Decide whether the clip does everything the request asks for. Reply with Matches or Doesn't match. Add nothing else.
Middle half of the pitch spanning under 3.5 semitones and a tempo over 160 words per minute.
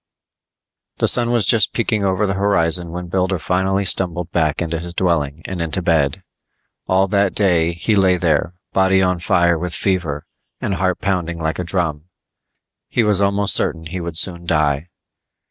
Matches